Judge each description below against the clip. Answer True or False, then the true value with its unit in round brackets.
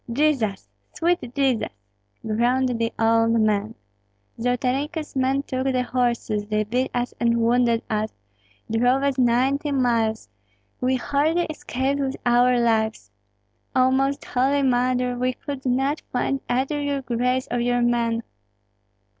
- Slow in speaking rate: True (130 wpm)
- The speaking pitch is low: False (250 Hz)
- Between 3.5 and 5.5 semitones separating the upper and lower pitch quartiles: False (2.5 semitones)